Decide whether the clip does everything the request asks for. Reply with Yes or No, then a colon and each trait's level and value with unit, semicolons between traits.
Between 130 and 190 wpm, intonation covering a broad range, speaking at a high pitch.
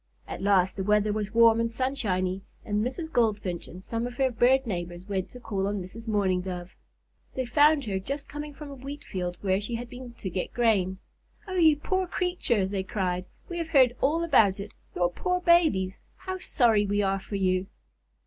No: average, 200 wpm; wide, 5.9 semitones; high, 215 Hz